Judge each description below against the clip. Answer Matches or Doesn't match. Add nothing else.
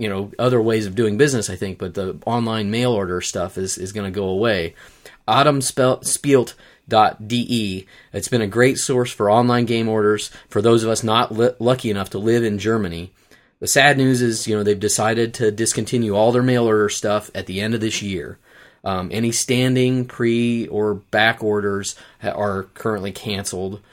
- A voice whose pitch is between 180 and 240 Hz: Doesn't match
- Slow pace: Doesn't match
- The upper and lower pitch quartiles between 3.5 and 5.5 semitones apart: Doesn't match